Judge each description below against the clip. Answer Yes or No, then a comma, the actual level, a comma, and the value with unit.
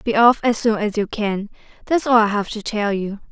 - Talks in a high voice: Yes, high, 215 Hz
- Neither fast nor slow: No, fast, 255 wpm